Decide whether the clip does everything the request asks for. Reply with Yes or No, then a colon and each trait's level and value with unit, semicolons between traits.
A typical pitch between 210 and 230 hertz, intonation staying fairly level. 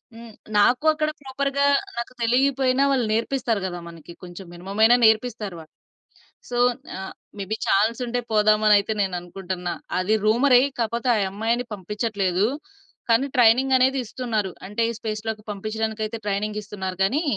No: high, 220 Hz; average, 3.5 semitones